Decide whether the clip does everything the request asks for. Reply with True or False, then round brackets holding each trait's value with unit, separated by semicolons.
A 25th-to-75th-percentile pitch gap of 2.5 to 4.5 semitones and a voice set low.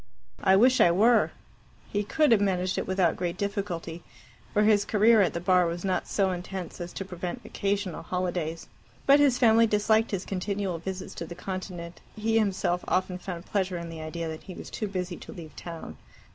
False (2.9 semitones; 185 Hz)